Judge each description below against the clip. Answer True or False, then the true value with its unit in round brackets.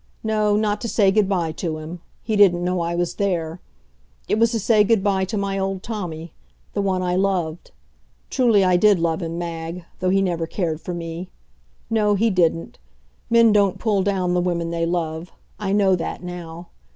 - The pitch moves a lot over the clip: False (3.2 semitones)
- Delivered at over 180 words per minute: True (195 wpm)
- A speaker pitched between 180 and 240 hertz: True (185 Hz)